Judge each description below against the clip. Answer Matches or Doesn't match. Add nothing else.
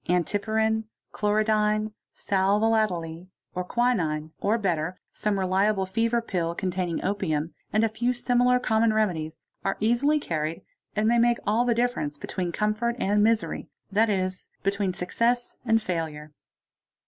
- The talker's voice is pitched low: Doesn't match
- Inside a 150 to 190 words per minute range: Doesn't match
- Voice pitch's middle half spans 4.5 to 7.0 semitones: Doesn't match